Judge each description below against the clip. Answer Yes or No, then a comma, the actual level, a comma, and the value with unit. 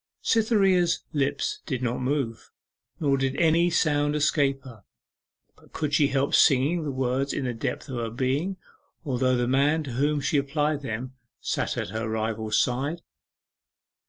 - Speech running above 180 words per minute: No, average, 160 wpm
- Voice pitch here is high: No, medium, 140 Hz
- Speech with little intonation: No, average, 3.1 semitones